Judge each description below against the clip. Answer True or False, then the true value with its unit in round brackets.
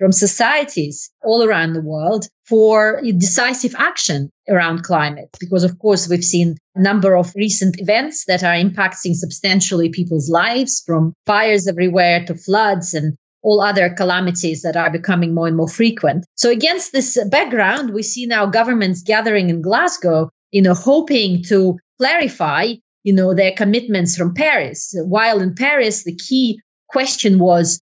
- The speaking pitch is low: False (190 Hz)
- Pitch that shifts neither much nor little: True (4.2 semitones)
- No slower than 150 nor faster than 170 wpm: True (155 wpm)